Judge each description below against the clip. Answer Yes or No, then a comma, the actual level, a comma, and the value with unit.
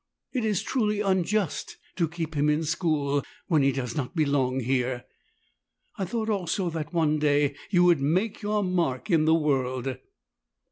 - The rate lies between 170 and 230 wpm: No, average, 160 wpm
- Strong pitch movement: No, average, 4.8 semitones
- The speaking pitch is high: No, medium, 160 Hz